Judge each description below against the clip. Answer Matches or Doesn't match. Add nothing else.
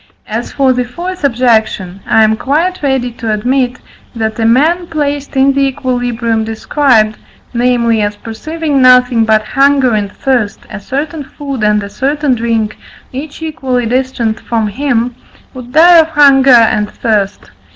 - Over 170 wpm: Doesn't match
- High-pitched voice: Matches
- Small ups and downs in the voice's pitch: Doesn't match